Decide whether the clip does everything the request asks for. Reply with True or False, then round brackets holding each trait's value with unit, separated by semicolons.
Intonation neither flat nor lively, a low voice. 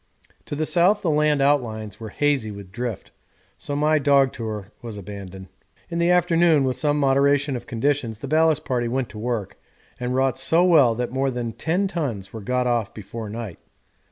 True (4.8 semitones; 130 Hz)